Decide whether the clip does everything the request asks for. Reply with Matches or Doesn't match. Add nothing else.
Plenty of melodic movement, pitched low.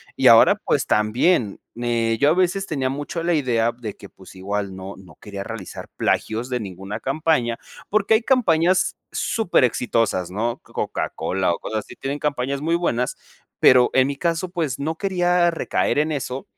Matches